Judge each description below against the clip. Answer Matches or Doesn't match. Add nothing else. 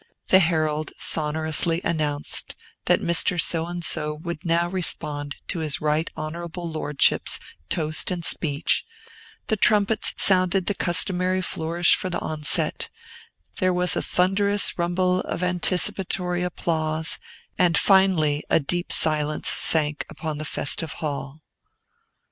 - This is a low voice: Doesn't match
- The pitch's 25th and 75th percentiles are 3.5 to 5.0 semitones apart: Doesn't match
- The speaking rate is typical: Doesn't match